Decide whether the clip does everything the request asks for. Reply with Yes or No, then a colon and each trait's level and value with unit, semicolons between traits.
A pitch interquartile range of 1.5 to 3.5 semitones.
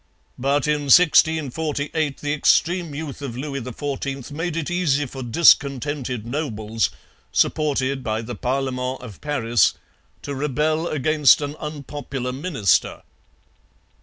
Yes: average, 3.0 semitones